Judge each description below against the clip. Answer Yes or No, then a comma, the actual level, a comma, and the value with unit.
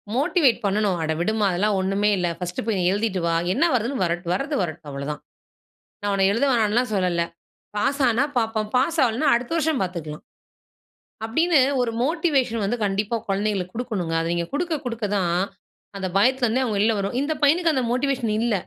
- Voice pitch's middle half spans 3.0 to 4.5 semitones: No, average, 5.2 semitones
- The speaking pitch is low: No, high, 220 Hz